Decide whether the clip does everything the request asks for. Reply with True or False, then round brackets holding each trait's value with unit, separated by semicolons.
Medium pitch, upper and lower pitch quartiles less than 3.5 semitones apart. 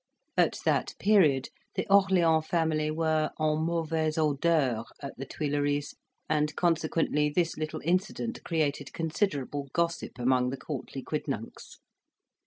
True (155 Hz; 2.5 semitones)